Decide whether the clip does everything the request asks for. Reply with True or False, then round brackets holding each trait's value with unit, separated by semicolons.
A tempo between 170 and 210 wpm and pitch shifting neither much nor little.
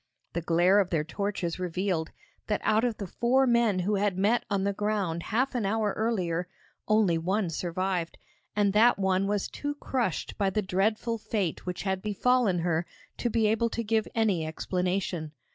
True (180 wpm; 3.5 semitones)